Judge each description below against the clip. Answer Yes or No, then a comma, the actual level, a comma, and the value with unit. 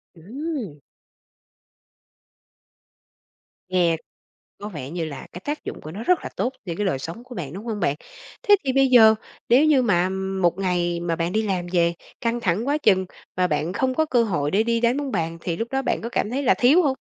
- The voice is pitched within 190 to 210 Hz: Yes, high, 205 Hz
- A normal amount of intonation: No, wide, 6.7 semitones